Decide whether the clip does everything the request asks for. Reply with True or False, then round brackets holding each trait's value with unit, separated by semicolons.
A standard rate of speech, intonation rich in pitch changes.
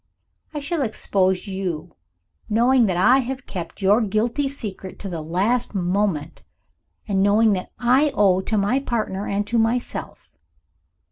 False (145 wpm; 4.3 semitones)